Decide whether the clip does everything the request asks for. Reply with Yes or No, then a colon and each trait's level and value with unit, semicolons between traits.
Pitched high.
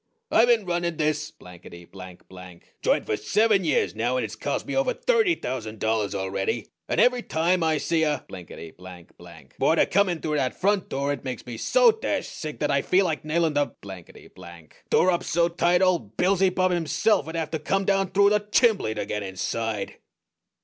No: medium, 155 Hz